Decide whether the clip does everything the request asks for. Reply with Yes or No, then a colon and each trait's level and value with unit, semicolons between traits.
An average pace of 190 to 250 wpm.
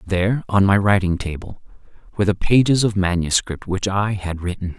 No: average, 175 wpm